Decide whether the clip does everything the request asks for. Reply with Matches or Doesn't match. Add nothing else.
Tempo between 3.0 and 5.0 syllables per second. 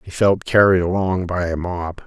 Matches